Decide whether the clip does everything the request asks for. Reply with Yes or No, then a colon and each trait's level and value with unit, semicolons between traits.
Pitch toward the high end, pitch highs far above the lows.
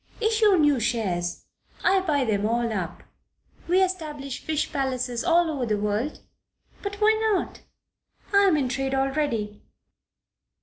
Yes: very high, 270 Hz; wide, 7.0 semitones